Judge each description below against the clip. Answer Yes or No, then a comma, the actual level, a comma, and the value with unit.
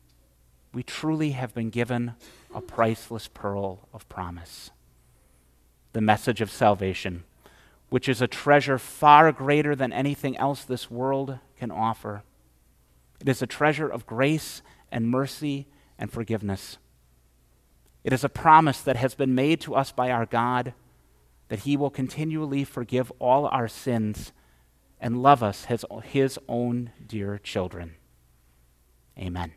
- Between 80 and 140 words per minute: Yes, slow, 135 wpm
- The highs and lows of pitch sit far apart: Yes, wide, 7.7 semitones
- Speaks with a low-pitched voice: Yes, low, 115 Hz